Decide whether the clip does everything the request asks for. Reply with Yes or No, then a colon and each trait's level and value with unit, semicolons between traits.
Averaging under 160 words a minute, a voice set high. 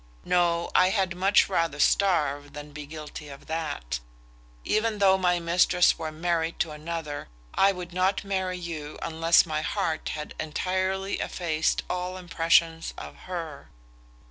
No: average, 145 wpm; medium, 170 Hz